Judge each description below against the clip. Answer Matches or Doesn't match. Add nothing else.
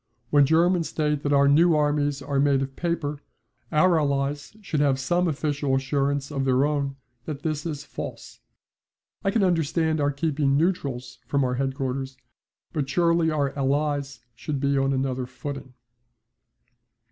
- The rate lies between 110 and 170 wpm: Matches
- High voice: Doesn't match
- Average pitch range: Doesn't match